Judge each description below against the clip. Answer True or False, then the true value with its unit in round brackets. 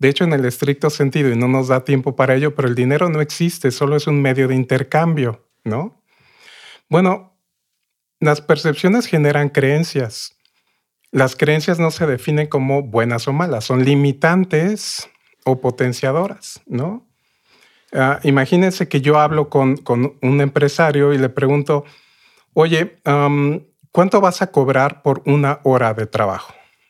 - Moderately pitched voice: True (145 Hz)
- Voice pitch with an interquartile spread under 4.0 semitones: True (3.1 semitones)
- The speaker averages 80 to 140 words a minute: False (150 wpm)